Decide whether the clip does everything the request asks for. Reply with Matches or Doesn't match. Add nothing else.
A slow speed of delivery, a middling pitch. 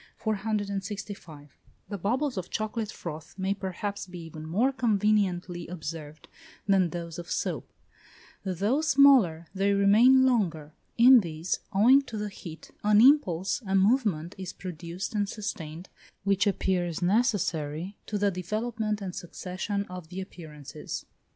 Doesn't match